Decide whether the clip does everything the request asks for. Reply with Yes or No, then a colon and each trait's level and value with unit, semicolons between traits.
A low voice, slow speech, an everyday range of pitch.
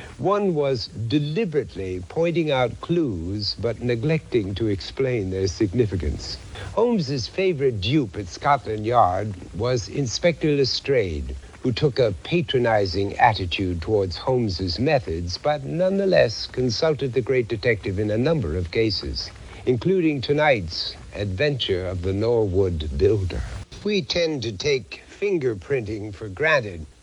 No: low, 115 Hz; slow, 120 wpm; wide, 7.2 semitones